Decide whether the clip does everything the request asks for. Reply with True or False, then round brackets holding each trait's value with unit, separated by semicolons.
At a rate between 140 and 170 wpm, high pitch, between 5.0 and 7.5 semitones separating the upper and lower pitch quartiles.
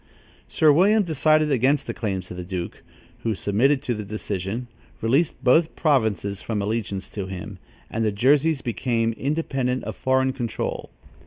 False (155 wpm; 120 Hz; 5.5 semitones)